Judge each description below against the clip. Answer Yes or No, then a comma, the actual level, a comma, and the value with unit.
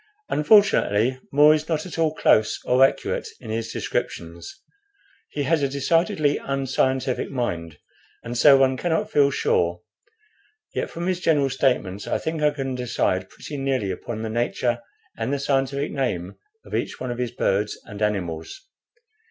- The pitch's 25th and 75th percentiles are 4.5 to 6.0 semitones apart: Yes, average, 4.9 semitones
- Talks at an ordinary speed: Yes, average, 160 wpm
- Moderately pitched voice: No, low, 130 Hz